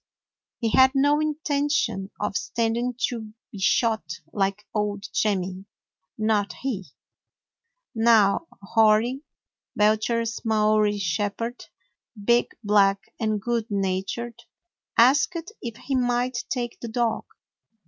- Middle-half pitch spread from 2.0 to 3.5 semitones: Yes, average, 2.9 semitones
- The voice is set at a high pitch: Yes, high, 225 Hz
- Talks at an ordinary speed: No, slow, 105 wpm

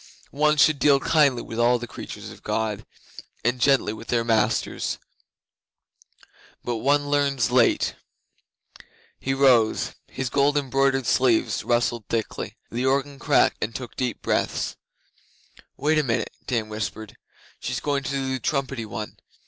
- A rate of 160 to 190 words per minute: No, average, 145 wpm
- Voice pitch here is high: No, low, 130 Hz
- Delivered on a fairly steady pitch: No, average, 3.1 semitones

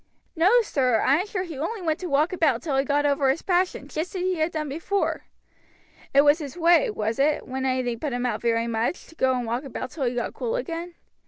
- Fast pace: Yes, fast, 250 wpm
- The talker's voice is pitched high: Yes, very high, 290 Hz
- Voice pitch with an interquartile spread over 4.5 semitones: Yes, average, 5.0 semitones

